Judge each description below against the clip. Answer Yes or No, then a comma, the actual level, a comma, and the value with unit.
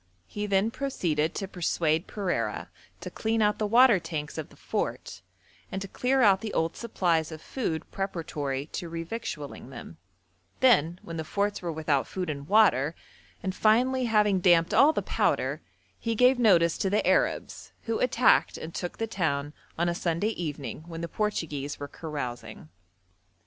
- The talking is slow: No, average, 165 wpm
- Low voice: No, medium, 175 Hz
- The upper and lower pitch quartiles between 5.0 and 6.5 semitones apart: Yes, wide, 5.4 semitones